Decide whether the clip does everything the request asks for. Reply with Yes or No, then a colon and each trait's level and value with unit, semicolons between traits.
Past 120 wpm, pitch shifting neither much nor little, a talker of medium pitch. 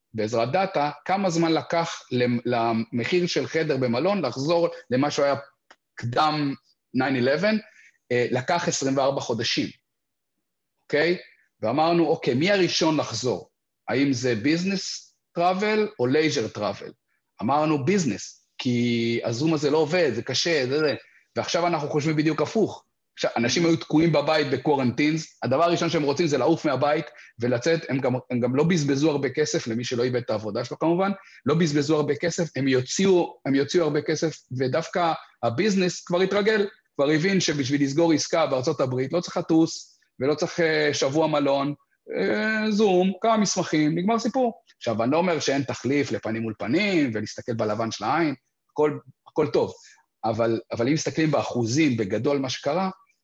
Yes: fast, 150 wpm; average, 4.9 semitones; medium, 150 Hz